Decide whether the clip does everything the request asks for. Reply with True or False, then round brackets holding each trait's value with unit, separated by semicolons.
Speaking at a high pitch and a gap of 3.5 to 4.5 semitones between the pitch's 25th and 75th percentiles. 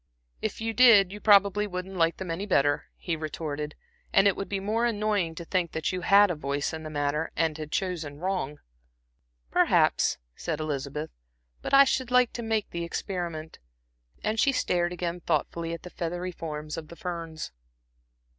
False (175 Hz; 4.2 semitones)